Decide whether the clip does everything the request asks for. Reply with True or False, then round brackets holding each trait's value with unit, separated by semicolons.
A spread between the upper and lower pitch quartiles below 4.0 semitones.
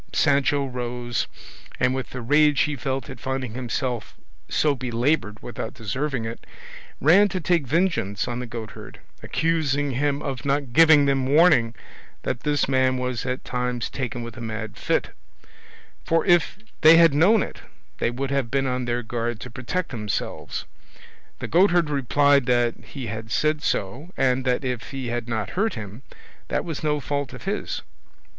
True (3.6 semitones)